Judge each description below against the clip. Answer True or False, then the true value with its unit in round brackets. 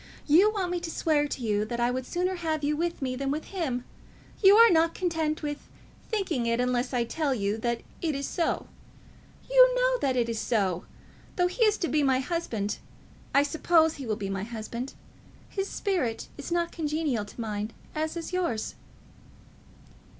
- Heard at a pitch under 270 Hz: False (295 Hz)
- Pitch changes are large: True (6.4 semitones)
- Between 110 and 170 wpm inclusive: False (185 wpm)